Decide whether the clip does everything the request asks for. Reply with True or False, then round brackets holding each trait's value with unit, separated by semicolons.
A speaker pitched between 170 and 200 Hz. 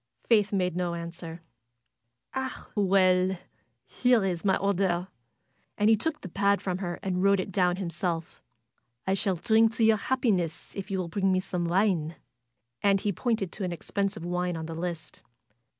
True (190 Hz)